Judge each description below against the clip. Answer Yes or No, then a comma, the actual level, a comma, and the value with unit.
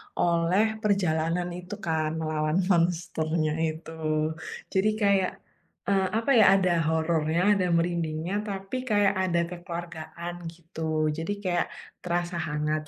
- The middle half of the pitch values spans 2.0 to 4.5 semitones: Yes, average, 3.0 semitones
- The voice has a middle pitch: Yes, medium, 170 Hz